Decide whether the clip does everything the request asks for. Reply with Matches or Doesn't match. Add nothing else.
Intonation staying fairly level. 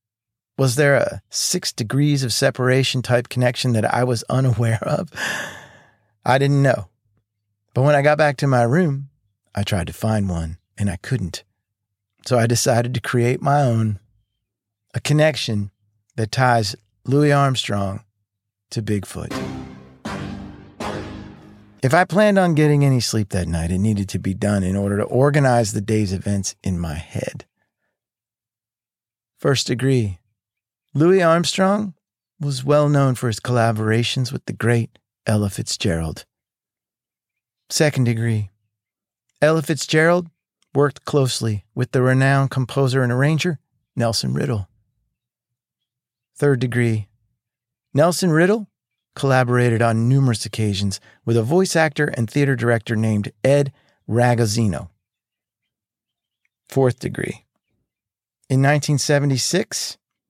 Doesn't match